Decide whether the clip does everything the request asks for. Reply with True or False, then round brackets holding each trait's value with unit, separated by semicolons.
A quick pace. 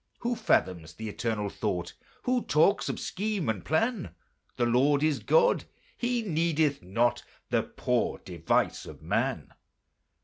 False (135 wpm)